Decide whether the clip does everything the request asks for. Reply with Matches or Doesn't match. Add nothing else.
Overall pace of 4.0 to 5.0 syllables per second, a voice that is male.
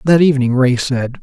Doesn't match